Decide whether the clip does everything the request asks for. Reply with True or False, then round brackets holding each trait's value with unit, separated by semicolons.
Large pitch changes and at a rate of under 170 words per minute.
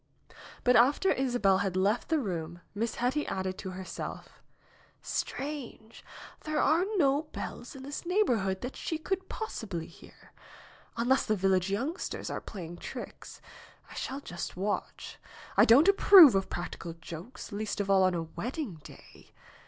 True (7.2 semitones; 155 wpm)